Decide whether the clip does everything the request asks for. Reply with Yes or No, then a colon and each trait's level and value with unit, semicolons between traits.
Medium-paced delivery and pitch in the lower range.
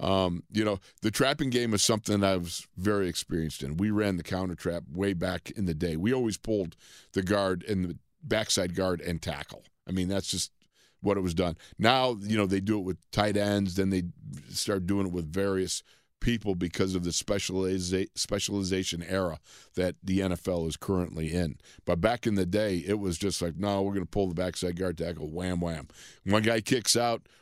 No: fast, 210 wpm; very low, 95 Hz